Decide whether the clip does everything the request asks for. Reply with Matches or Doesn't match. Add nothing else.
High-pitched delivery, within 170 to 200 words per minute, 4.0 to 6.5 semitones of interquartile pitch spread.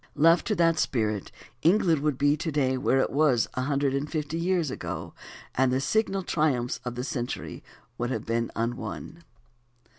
Doesn't match